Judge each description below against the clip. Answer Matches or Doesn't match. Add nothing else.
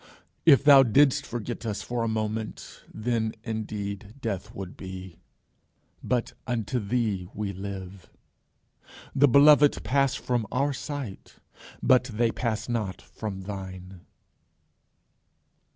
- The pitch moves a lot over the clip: Doesn't match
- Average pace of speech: Doesn't match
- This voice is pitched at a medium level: Doesn't match